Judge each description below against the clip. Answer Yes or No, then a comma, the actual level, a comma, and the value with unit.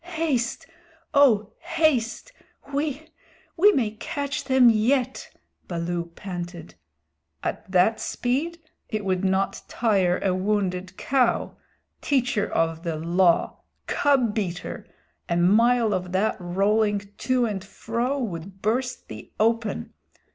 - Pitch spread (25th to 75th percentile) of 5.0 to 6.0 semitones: Yes, average, 5.3 semitones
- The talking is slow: Yes, slow, 115 wpm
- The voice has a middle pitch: No, high, 215 Hz